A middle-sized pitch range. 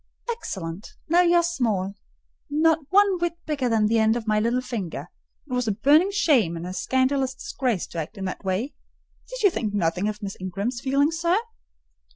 No: wide, 8.0 semitones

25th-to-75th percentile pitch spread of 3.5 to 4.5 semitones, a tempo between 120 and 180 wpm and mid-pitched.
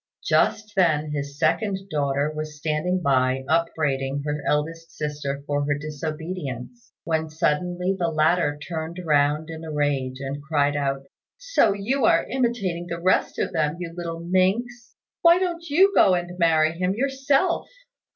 Yes: average, 4.1 semitones; average, 150 wpm; medium, 160 Hz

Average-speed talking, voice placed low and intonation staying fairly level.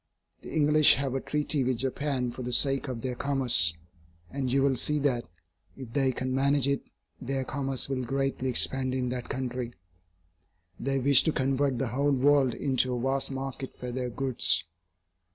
Yes: average, 175 wpm; low, 130 Hz; narrow, 1.6 semitones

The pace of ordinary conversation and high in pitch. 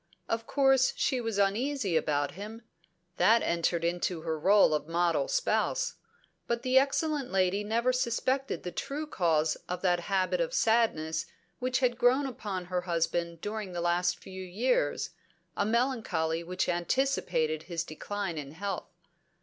Yes: average, 150 wpm; high, 195 Hz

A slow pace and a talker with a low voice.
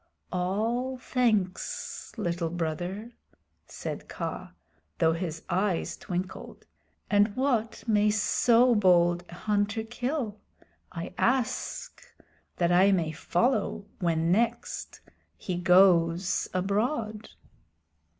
No: slow, 95 wpm; high, 200 Hz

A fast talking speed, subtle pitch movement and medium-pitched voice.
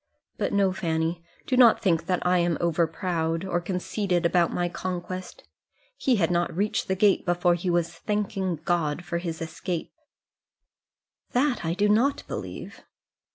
No: average, 155 wpm; narrow, 2.2 semitones; medium, 175 Hz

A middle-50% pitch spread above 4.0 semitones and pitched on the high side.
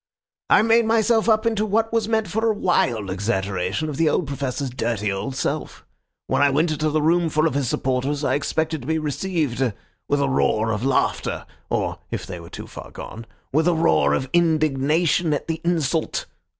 No: average, 5.3 semitones; medium, 150 Hz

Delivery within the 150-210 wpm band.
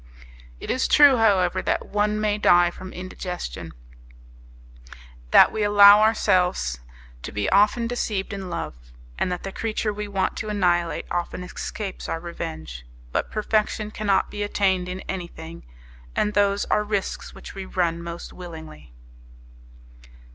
No: average, 140 wpm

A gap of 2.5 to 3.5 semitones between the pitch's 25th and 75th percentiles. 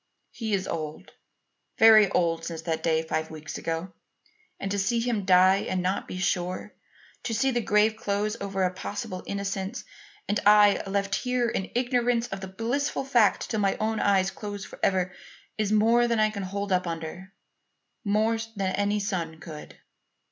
Yes: average, 2.9 semitones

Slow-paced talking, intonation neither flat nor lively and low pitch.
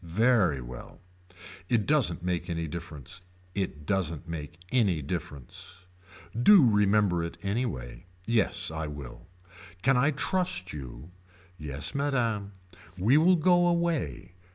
No: slow, 125 wpm; wide, 7.9 semitones; very low, 95 Hz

